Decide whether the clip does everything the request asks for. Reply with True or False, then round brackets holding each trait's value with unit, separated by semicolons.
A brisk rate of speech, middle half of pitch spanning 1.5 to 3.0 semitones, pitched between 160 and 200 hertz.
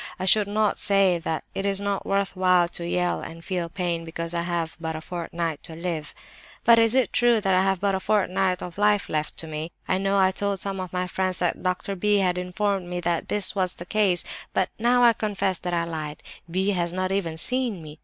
True (235 wpm; 2.7 semitones; 185 Hz)